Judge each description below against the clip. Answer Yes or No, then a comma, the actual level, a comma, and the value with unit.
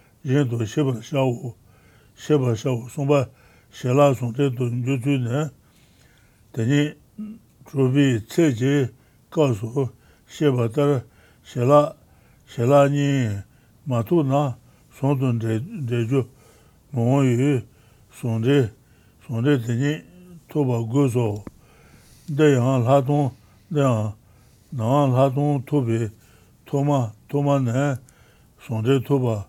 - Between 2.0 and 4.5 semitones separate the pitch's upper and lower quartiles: Yes, average, 3.4 semitones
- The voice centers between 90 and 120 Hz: No, low, 130 Hz